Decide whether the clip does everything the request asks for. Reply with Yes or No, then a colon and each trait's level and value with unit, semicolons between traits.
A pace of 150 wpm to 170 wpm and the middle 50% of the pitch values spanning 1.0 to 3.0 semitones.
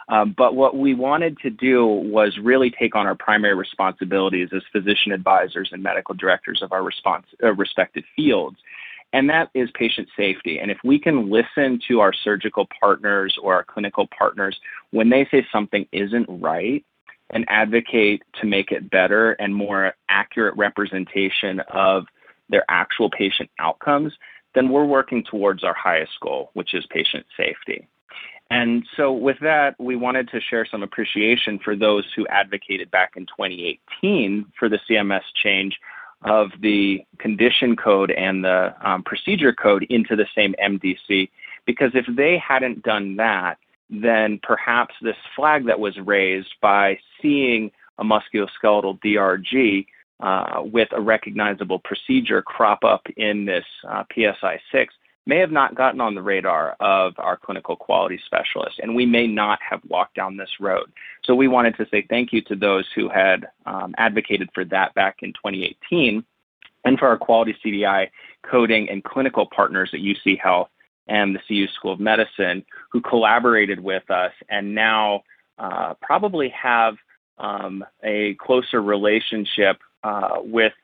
No: average, 155 wpm; average, 3.4 semitones